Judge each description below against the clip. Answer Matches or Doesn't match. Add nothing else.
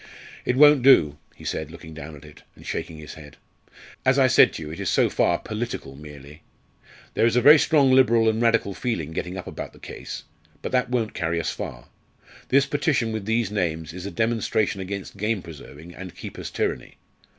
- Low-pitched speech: Matches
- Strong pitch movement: Matches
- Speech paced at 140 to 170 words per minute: Doesn't match